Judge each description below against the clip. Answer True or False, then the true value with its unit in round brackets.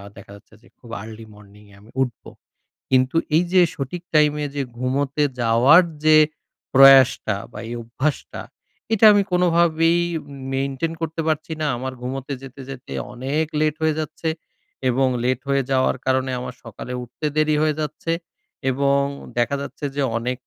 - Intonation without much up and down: False (3.5 semitones)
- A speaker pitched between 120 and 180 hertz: True (135 Hz)